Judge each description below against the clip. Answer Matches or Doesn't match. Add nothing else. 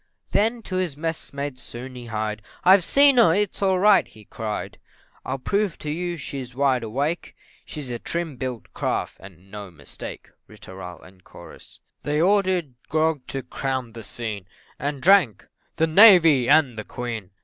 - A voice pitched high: Doesn't match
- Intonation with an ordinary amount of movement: Doesn't match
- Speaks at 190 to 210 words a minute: Doesn't match